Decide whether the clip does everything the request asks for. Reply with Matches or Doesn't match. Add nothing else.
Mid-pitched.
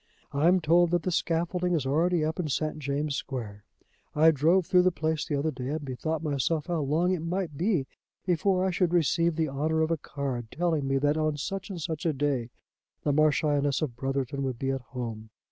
Matches